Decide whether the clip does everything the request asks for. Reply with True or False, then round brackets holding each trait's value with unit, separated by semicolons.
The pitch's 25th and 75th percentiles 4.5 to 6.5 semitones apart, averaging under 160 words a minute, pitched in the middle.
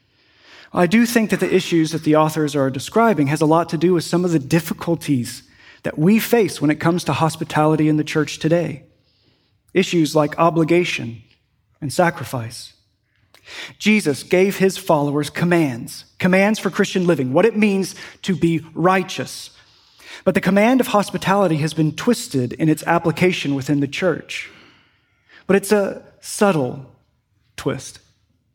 True (5.0 semitones; 150 wpm; 160 Hz)